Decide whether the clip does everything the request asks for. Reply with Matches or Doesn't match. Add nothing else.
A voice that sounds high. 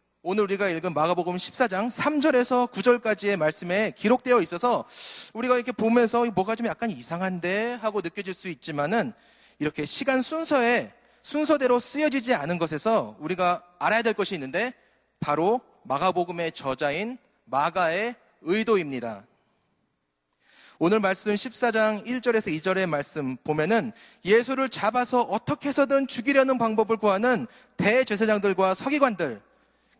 Matches